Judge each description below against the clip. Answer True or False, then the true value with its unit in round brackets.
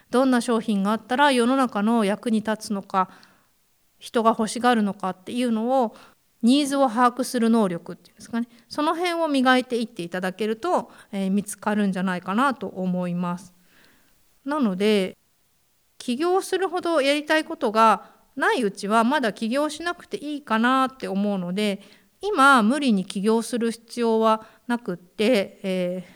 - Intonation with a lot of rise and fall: False (4.5 semitones)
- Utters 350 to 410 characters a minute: False (330 characters per minute)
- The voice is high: True (225 Hz)